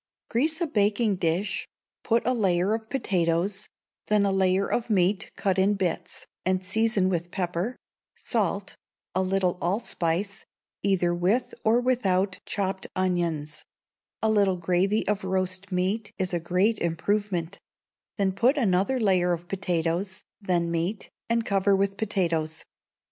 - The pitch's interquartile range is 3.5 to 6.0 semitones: No, average, 2.8 semitones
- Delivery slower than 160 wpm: Yes, average, 140 wpm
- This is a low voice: No, high, 190 Hz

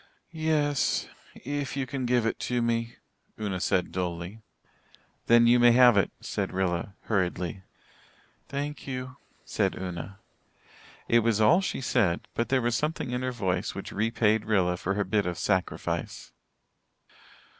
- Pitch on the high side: No, low, 115 Hz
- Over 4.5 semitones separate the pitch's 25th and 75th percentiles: Yes, average, 5.0 semitones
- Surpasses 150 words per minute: No, average, 145 wpm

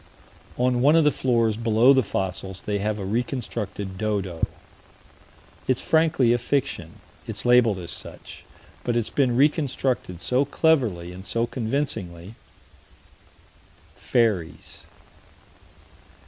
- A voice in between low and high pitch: No, low, 115 Hz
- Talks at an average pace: No, slow, 115 wpm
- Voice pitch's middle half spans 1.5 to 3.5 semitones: No, average, 5.0 semitones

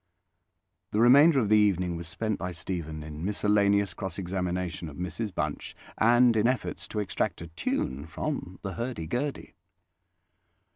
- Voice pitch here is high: No, very low, 95 Hz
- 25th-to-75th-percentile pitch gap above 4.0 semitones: Yes, average, 4.6 semitones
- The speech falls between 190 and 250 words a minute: No, average, 150 wpm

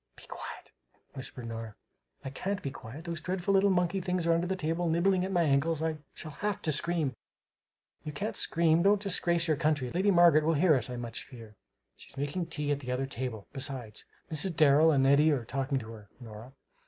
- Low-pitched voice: No, medium, 155 Hz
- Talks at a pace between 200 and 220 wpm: Yes, fast, 205 wpm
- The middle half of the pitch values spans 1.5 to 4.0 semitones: No, average, 4.7 semitones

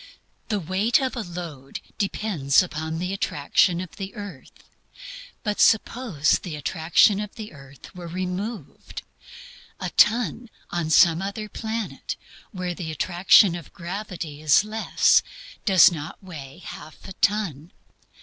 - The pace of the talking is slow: Yes, slow, 130 wpm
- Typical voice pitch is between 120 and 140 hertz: No, medium, 180 Hz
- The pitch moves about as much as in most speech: Yes, average, 4.6 semitones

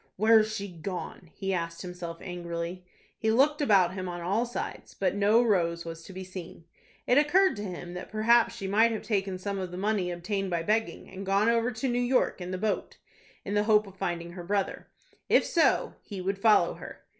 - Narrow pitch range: No, average, 3.6 semitones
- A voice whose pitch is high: Yes, high, 195 Hz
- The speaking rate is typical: No, fast, 210 wpm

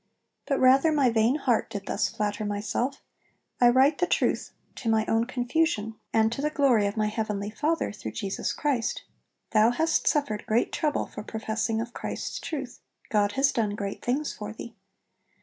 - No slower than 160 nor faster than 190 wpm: Yes, average, 175 wpm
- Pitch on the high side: Yes, high, 230 Hz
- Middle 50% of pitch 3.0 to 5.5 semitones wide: Yes, average, 4.3 semitones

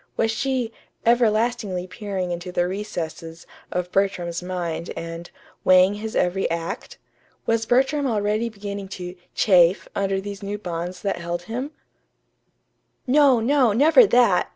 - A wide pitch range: No, average, 4.3 semitones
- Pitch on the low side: No, high, 200 Hz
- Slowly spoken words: Yes, slow, 130 wpm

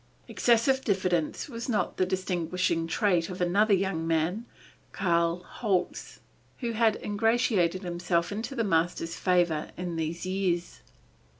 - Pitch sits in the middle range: Yes, medium, 180 Hz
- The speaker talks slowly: Yes, slow, 125 wpm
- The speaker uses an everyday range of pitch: Yes, average, 3.7 semitones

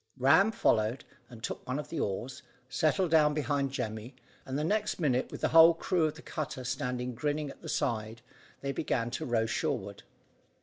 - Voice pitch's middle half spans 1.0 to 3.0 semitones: No, average, 4.6 semitones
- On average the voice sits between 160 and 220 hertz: No, low, 135 Hz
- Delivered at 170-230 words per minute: Yes, average, 185 wpm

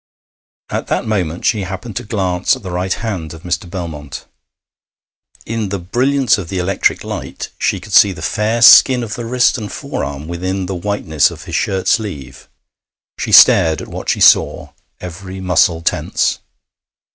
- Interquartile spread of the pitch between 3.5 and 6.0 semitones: Yes, average, 4.0 semitones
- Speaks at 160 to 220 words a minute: Yes, average, 170 wpm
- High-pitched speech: No, very low, 95 Hz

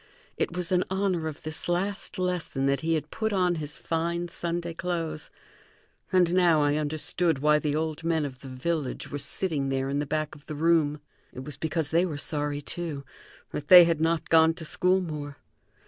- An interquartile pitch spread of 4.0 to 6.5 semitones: No, average, 2.8 semitones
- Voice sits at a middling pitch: Yes, medium, 160 Hz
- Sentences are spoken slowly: No, average, 195 wpm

